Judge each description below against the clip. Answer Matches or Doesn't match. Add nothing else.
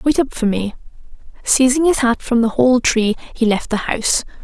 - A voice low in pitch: Doesn't match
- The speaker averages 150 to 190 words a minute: Doesn't match